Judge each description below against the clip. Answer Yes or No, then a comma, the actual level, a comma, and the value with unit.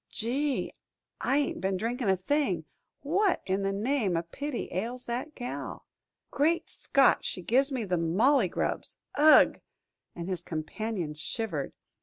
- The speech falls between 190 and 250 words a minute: No, average, 150 wpm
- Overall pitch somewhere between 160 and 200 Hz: No, high, 230 Hz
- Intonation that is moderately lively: No, wide, 7.0 semitones